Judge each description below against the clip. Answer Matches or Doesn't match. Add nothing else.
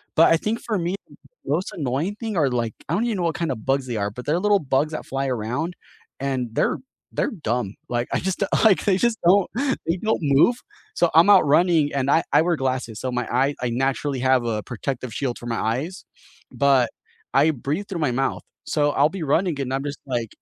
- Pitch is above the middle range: Doesn't match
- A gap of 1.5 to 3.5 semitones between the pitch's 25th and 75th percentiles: Doesn't match